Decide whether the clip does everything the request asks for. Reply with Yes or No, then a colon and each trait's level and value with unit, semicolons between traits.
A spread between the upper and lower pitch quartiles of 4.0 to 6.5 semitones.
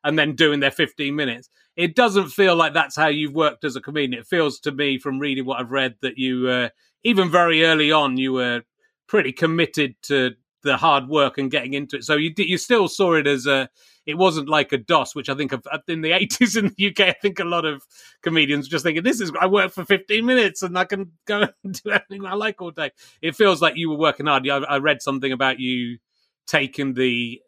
Yes: average, 5.0 semitones